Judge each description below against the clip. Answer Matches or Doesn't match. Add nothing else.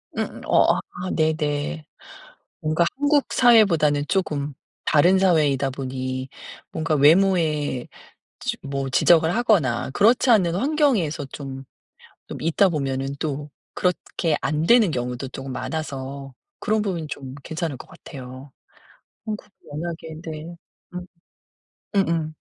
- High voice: Doesn't match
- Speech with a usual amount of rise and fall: Matches